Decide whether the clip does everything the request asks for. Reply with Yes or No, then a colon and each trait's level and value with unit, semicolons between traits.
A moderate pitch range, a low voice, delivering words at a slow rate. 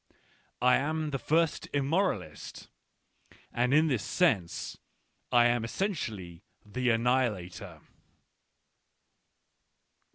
No: wide, 6.4 semitones; low, 125 Hz; slow, 70 wpm